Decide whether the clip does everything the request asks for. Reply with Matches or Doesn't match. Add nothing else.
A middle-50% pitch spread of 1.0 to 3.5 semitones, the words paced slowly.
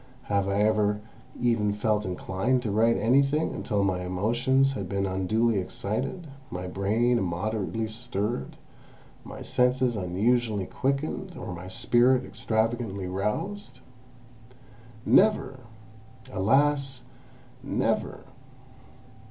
Doesn't match